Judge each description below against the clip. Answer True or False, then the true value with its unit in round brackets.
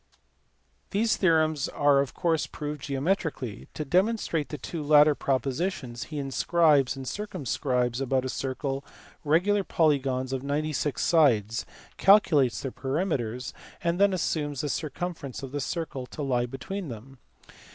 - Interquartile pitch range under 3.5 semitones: False (3.8 semitones)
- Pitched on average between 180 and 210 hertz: False (145 Hz)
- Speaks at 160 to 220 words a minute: False (145 wpm)